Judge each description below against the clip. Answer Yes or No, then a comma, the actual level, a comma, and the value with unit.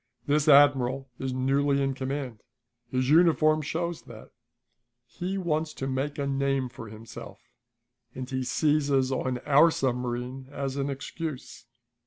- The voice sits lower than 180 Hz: Yes, low, 135 Hz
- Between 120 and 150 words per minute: Yes, slow, 135 wpm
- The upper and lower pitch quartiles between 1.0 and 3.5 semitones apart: Yes, narrow, 2.4 semitones